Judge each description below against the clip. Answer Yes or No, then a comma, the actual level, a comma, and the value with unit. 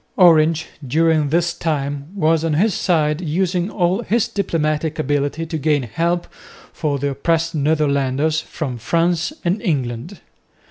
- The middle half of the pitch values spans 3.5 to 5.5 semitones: No, average, 2.9 semitones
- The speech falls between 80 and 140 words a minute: Yes, slow, 135 wpm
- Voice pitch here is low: No, medium, 160 Hz